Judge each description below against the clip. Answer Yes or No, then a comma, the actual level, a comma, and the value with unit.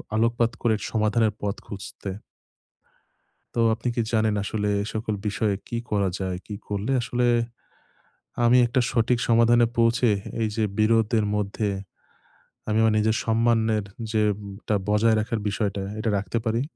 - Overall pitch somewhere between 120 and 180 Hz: No, low, 110 Hz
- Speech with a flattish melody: Yes, narrow, 1.8 semitones